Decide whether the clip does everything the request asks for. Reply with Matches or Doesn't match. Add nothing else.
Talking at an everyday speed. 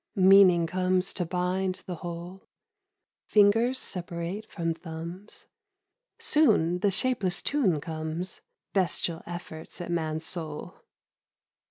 Doesn't match